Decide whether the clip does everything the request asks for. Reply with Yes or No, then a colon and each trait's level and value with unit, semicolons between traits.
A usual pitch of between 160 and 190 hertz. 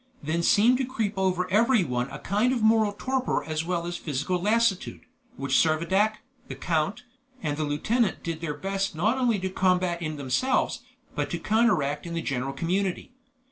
Yes: medium, 185 Hz